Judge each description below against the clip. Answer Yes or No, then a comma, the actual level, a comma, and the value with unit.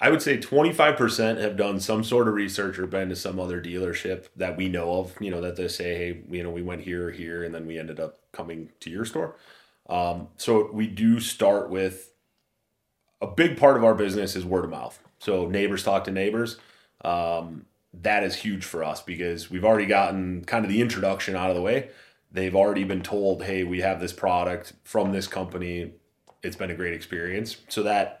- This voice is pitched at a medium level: No, very low, 95 Hz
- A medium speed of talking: No, fast, 210 wpm